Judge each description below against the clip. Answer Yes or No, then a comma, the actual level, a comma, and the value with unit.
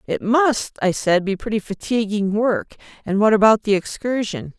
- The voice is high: Yes, high, 210 Hz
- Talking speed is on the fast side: No, average, 170 wpm